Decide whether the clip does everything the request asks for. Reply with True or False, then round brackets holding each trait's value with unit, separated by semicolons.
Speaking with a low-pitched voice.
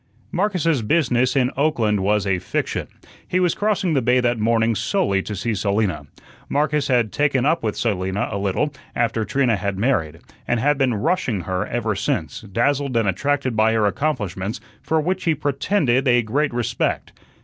True (120 Hz)